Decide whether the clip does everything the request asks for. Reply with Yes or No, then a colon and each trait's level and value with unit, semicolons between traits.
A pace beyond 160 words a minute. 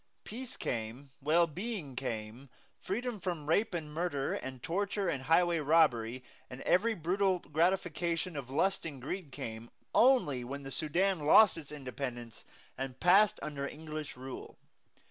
No: average, 145 wpm